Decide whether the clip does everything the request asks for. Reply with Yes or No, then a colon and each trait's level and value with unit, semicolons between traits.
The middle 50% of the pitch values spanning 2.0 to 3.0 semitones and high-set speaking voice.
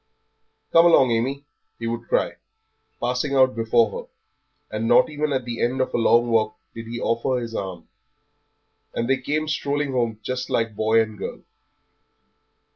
No: average, 2.7 semitones; low, 120 Hz